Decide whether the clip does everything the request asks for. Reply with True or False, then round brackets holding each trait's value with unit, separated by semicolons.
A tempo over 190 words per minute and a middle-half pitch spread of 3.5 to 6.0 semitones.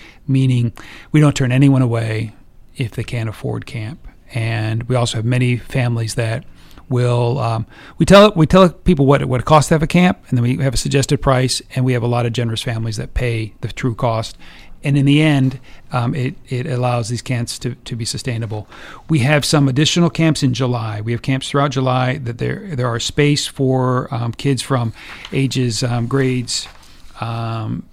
False (200 wpm; 2.7 semitones)